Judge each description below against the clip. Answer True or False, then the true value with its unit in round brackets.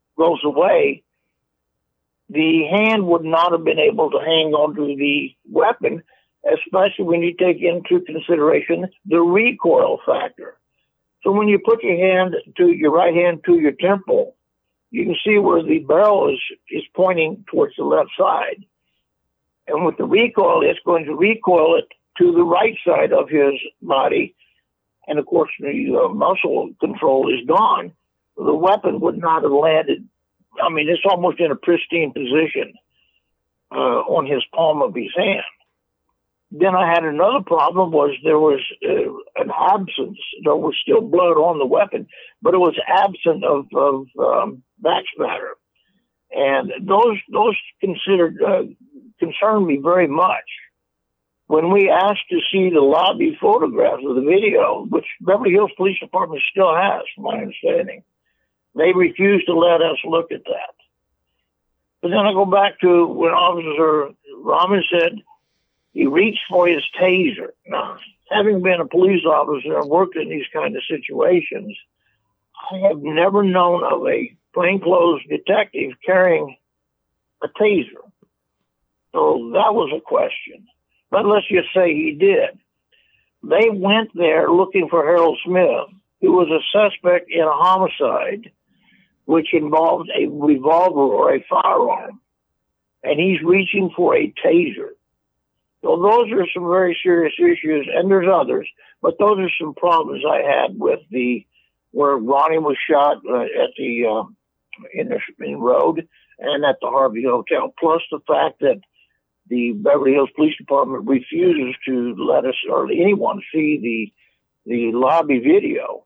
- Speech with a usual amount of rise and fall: False (7.1 semitones)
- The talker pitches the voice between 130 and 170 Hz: False (180 Hz)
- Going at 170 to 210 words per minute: False (150 wpm)